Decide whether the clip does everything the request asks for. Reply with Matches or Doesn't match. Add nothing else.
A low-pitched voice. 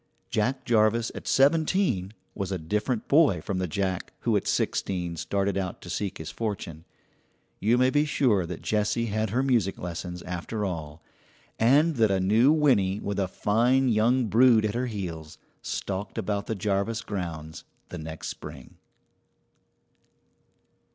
Matches